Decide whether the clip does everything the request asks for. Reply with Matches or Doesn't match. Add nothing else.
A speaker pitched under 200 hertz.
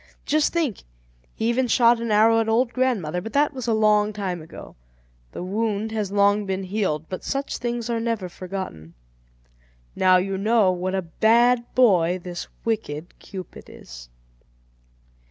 Doesn't match